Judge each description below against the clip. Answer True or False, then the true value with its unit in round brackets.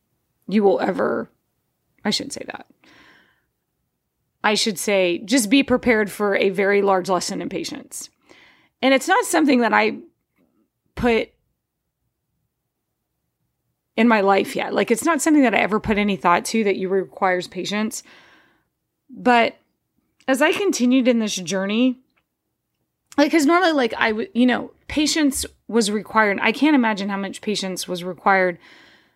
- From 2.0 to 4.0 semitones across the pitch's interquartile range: False (4.8 semitones)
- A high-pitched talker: True (220 Hz)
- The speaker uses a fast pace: False (150 wpm)